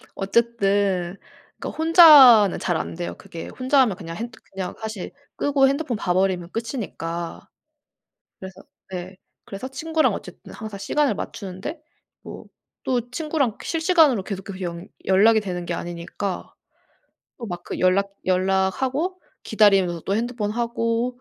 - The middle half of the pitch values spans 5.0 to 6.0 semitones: Yes, wide, 5.4 semitones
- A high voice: Yes, high, 205 Hz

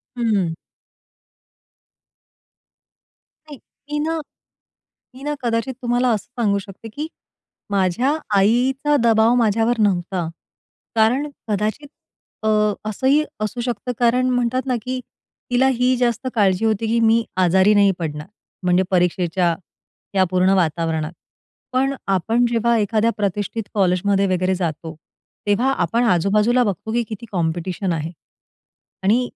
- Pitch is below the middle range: No, high, 215 Hz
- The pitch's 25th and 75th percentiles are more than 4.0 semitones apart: Yes, average, 4.6 semitones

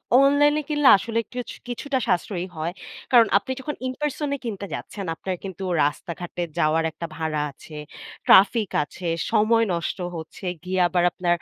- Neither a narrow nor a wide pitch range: No, wide, 6.4 semitones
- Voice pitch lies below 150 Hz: No, high, 195 Hz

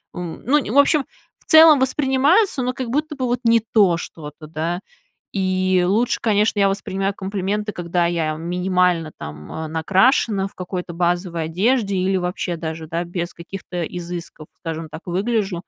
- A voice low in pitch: No, medium, 185 Hz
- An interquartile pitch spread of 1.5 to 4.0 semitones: No, average, 4.5 semitones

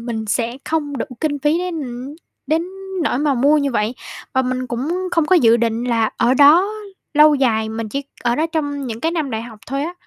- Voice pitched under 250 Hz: No, very high, 270 Hz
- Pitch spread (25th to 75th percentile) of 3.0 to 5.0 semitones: Yes, average, 4.5 semitones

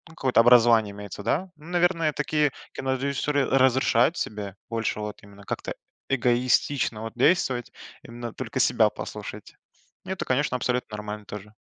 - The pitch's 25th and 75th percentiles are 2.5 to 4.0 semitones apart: No, average, 4.6 semitones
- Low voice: Yes, low, 125 Hz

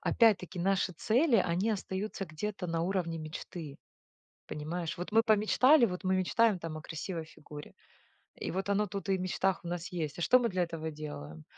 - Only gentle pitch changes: No, average, 3.6 semitones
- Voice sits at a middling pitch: Yes, medium, 180 Hz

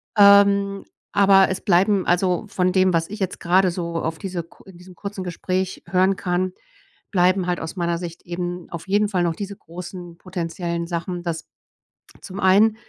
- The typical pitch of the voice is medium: Yes, medium, 180 Hz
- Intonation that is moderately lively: No, narrow, 2.0 semitones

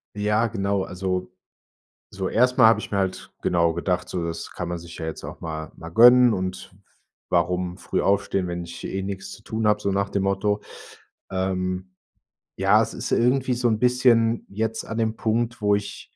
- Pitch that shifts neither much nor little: Yes, average, 3.4 semitones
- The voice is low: Yes, low, 100 Hz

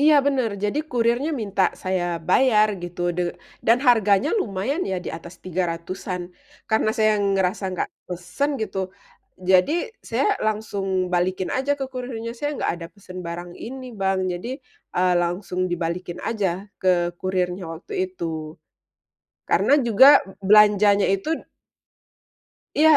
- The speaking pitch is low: No, high, 195 Hz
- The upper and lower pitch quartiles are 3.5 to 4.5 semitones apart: Yes, average, 4.2 semitones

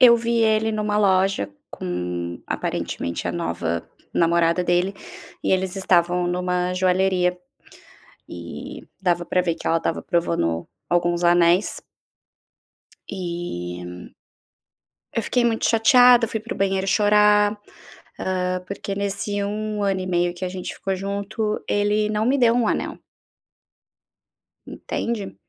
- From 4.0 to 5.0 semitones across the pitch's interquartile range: No, average, 3.4 semitones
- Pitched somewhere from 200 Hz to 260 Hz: No, high, 190 Hz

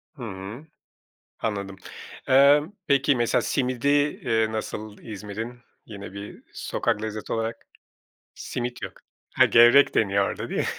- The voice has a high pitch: No, low, 115 Hz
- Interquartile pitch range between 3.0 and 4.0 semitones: Yes, average, 3.7 semitones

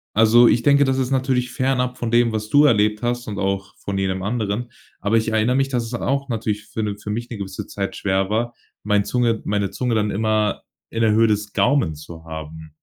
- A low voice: Yes, low, 110 Hz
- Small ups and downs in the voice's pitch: No, average, 3.3 semitones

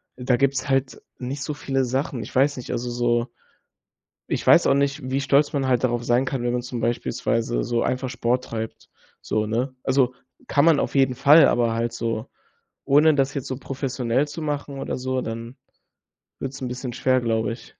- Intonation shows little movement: Yes, narrow, 2.3 semitones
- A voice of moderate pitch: No, low, 130 Hz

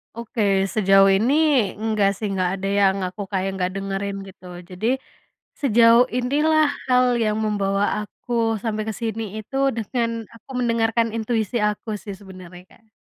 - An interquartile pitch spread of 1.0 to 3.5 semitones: Yes, average, 2.9 semitones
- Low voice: No, high, 215 Hz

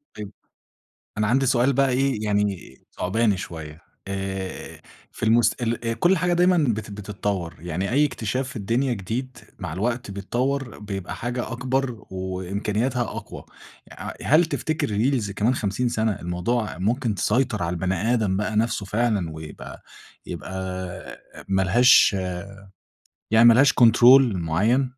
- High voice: No, low, 110 Hz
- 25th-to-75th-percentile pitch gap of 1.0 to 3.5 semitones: No, average, 4.4 semitones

